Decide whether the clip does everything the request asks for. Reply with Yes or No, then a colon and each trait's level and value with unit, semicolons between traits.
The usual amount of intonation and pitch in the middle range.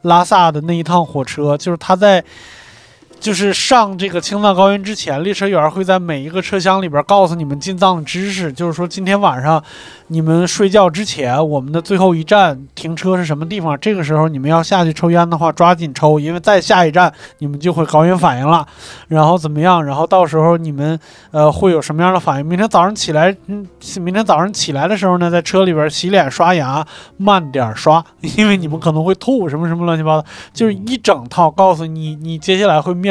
Yes: average, 3.5 semitones; medium, 175 Hz